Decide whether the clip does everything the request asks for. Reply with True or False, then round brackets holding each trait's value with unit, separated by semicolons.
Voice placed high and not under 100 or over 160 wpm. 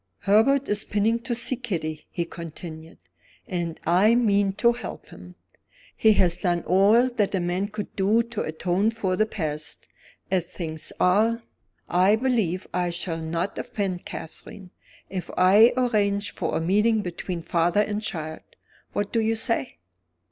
True (195 Hz; 155 wpm)